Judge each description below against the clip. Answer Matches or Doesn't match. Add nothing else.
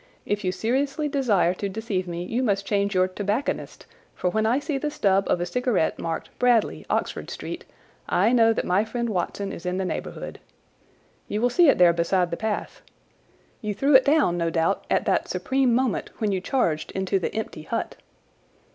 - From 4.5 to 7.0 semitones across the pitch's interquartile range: Matches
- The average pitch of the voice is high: Matches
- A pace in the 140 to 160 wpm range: Doesn't match